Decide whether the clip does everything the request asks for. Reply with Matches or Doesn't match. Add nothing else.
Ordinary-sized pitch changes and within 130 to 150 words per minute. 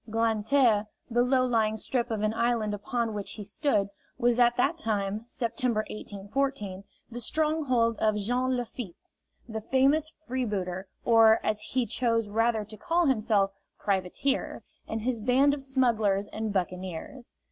Matches